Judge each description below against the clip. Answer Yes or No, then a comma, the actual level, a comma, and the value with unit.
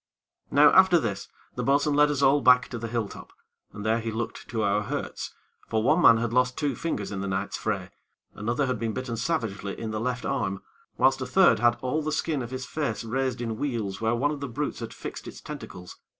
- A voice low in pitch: Yes, low, 120 Hz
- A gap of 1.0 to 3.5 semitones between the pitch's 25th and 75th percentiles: No, average, 4.1 semitones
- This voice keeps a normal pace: No, fast, 230 wpm